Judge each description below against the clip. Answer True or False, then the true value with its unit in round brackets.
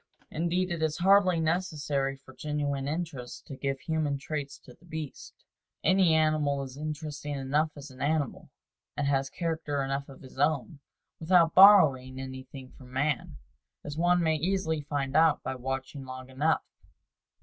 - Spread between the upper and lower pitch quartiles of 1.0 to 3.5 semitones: True (2.9 semitones)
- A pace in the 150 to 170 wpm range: True (155 wpm)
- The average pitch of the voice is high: False (145 Hz)